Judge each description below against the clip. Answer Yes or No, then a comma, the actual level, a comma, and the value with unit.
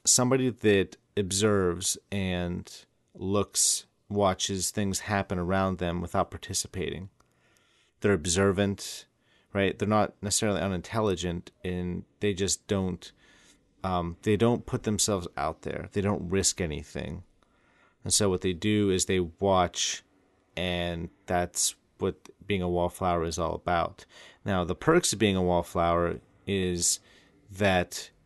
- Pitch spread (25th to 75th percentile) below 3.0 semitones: Yes, narrow, 2.4 semitones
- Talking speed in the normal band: No, slow, 125 wpm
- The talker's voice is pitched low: Yes, very low, 95 Hz